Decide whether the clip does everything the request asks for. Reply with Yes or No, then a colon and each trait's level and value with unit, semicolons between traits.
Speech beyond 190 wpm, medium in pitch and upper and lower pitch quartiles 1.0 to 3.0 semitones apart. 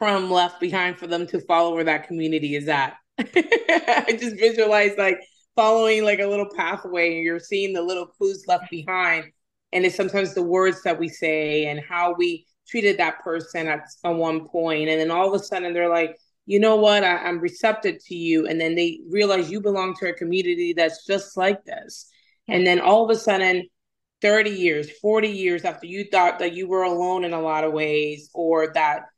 No: fast, 205 wpm; medium, 180 Hz; average, 3.4 semitones